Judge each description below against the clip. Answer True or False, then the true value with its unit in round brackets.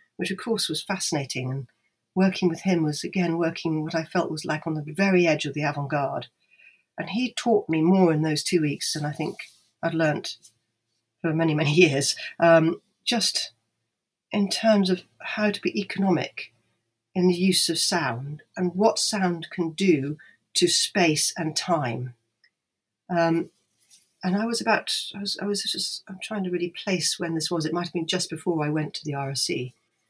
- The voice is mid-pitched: True (170 Hz)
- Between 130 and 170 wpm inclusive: False (185 wpm)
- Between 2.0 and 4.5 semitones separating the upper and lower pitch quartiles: True (3.8 semitones)